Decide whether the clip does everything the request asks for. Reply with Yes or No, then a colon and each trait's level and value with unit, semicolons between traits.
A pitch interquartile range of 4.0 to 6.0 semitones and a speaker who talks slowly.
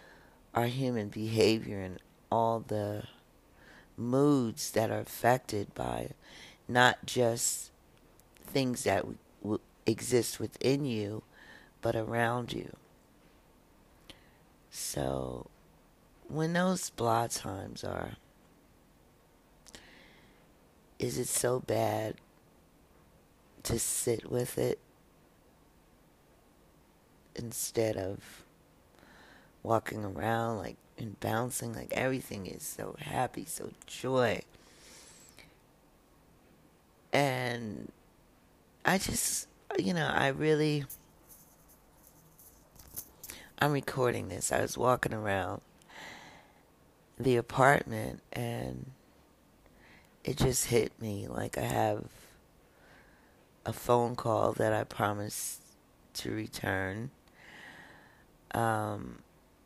No: average, 3.2 semitones; slow, 85 wpm